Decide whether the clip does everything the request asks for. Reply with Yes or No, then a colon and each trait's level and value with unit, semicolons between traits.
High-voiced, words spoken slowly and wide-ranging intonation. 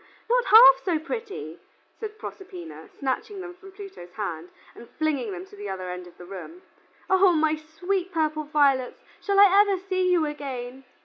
No: very high, 315 Hz; average, 175 wpm; wide, 7.6 semitones